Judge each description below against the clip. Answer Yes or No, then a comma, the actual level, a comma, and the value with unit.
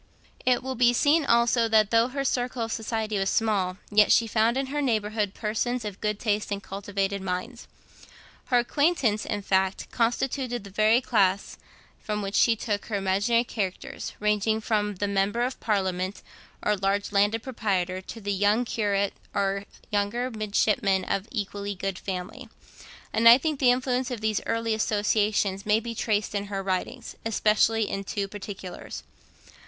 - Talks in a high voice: Yes, high, 210 Hz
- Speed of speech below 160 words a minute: No, average, 165 wpm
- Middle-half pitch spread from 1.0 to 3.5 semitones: Yes, average, 2.8 semitones